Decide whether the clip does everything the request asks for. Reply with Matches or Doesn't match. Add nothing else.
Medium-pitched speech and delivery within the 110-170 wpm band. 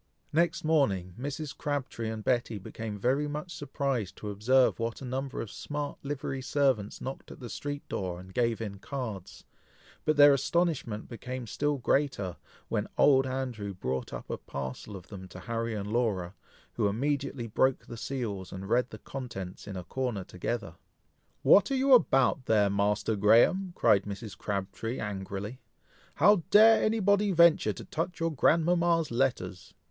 Doesn't match